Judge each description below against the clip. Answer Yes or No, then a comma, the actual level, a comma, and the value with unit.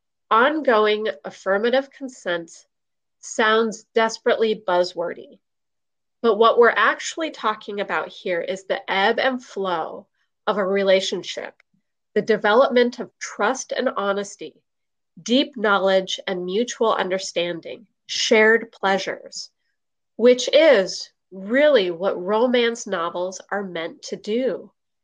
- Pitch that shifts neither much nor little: Yes, average, 3.7 semitones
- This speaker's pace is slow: Yes, slow, 105 wpm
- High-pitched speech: Yes, high, 215 Hz